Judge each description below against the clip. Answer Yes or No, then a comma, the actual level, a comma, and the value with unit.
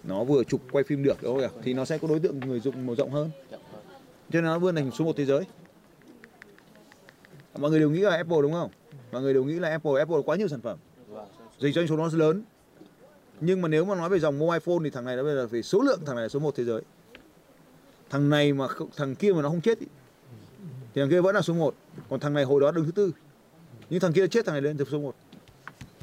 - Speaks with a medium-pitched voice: Yes, medium, 150 Hz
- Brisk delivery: Yes, fast, 265 wpm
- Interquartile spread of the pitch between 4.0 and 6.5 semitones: No, average, 3.5 semitones